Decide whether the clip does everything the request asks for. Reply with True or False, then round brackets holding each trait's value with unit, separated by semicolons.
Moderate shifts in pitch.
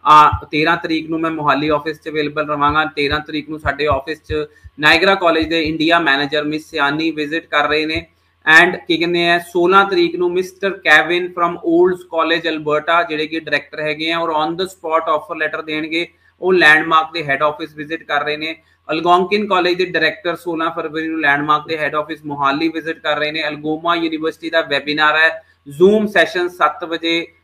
False (1.9 semitones)